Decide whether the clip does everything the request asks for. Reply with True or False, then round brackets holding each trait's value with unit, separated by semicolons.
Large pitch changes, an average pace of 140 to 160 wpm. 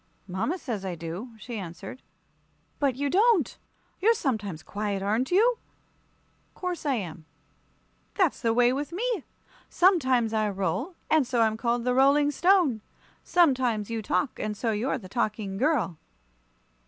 True (6.1 semitones; 145 wpm)